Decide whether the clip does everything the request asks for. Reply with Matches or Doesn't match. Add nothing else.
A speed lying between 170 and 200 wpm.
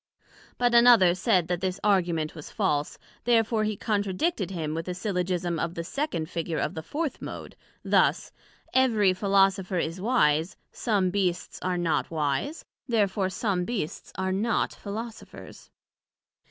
Doesn't match